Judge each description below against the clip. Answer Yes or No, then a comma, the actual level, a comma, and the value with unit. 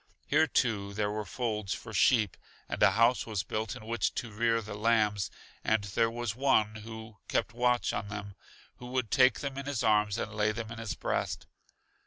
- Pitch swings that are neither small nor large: No, narrow, 2.1 semitones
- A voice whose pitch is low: Yes, low, 110 Hz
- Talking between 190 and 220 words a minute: Yes, average, 200 wpm